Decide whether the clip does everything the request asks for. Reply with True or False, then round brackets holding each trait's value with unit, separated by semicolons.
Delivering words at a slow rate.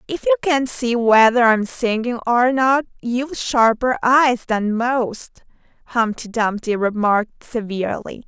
True (130 wpm)